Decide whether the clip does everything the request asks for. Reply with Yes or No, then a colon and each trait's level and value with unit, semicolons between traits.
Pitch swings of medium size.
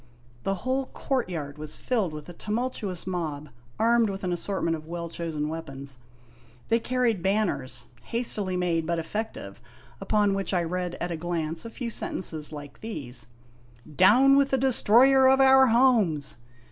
No: wide, 6.4 semitones